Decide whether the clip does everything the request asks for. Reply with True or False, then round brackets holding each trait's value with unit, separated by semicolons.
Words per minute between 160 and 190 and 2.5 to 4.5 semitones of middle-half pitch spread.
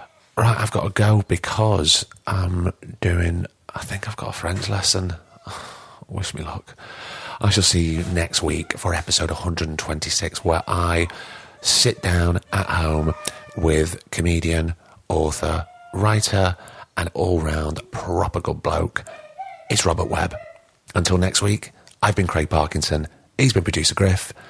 False (135 wpm; 4.2 semitones)